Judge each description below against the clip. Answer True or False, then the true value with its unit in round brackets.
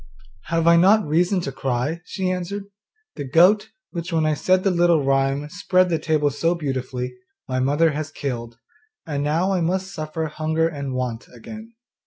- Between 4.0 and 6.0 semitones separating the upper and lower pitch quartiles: True (4.4 semitones)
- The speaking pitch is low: False (160 Hz)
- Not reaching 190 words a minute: True (175 wpm)